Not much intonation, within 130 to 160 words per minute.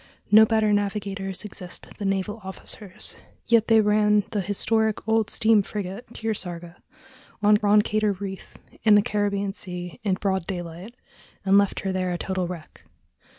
Yes: narrow, 2.1 semitones; average, 150 wpm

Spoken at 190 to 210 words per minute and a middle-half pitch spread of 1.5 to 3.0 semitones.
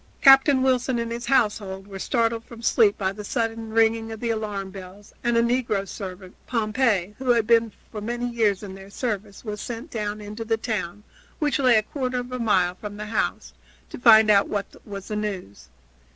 Yes: average, 200 wpm; average, 2.7 semitones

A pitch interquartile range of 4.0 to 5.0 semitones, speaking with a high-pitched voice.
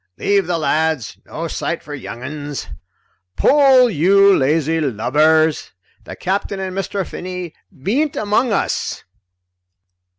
No: average, 4.7 semitones; medium, 170 Hz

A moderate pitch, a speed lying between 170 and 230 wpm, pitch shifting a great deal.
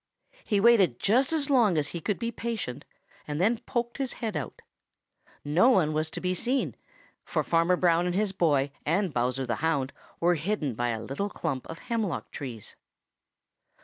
Yes: medium, 175 Hz; average, 180 wpm; wide, 7.1 semitones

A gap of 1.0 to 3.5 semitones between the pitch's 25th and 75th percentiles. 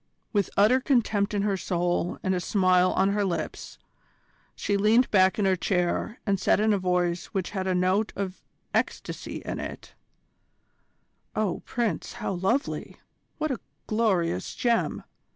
Yes: average, 2.8 semitones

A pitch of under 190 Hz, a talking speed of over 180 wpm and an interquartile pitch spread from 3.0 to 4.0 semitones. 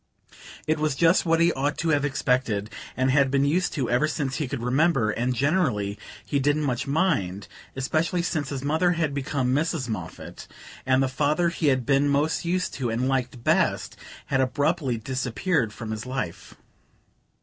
No: medium, 140 Hz; average, 175 wpm; average, 3.6 semitones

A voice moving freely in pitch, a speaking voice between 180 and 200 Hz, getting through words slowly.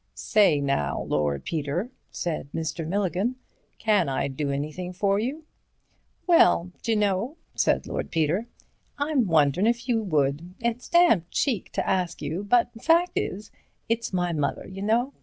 No: wide, 6.7 semitones; high, 190 Hz; average, 150 wpm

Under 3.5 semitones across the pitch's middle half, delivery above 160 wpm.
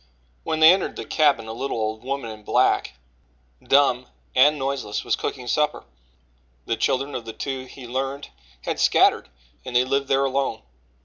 Yes: narrow, 2.4 semitones; average, 170 wpm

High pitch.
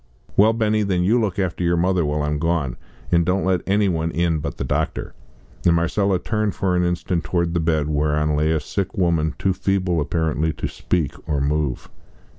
No: very low, 85 Hz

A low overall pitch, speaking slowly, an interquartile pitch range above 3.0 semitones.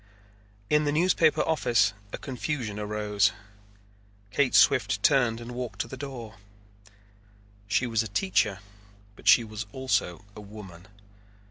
Yes: low, 115 Hz; slow, 130 wpm; average, 4.2 semitones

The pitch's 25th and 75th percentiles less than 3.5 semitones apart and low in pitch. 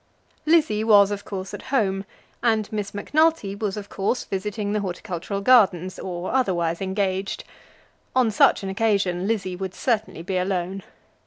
No: narrow, 2.4 semitones; high, 200 Hz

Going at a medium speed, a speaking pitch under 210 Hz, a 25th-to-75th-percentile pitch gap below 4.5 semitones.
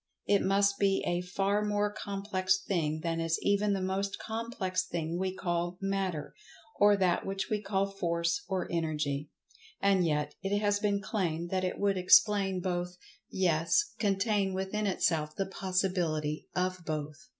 Yes: average, 150 wpm; high, 190 Hz; average, 2.8 semitones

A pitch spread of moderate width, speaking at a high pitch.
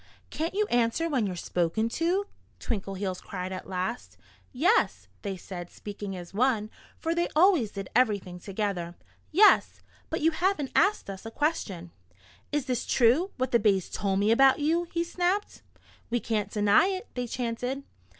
No: wide, 8.5 semitones; high, 235 Hz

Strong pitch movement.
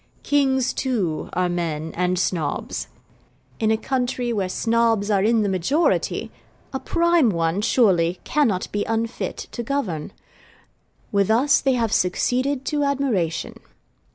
Yes: wide, 6.4 semitones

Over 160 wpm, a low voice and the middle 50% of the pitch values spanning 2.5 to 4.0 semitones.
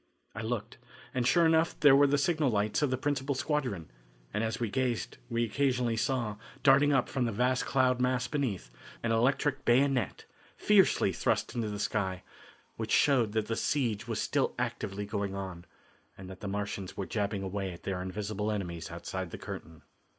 No: average, 180 wpm; low, 115 Hz; average, 4.8 semitones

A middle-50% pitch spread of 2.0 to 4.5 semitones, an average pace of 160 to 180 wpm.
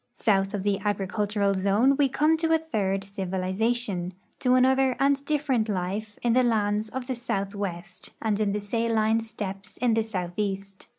Yes: average, 3.9 semitones; average, 165 wpm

